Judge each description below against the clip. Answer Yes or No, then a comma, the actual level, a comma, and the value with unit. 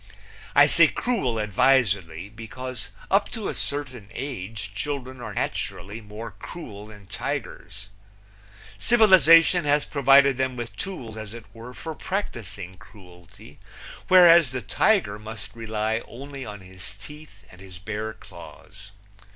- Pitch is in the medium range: No, low, 115 Hz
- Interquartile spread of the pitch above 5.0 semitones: Yes, wide, 5.5 semitones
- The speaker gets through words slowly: Yes, slow, 130 wpm